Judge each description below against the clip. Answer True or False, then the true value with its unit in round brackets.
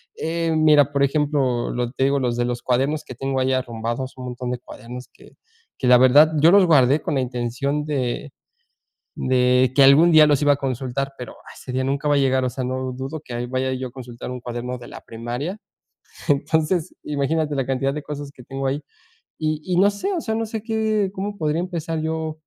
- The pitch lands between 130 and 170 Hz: True (135 Hz)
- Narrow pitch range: False (3.6 semitones)